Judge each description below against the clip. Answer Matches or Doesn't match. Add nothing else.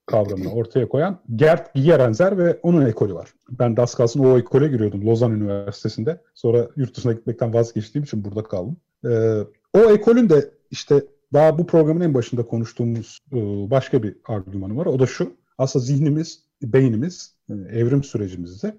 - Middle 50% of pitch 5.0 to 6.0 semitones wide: Matches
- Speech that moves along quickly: Matches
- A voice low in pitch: Matches